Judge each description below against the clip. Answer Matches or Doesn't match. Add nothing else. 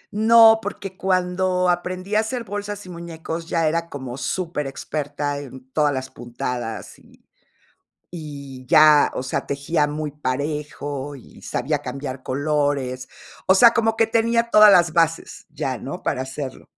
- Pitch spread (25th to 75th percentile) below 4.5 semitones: Doesn't match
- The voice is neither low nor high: Matches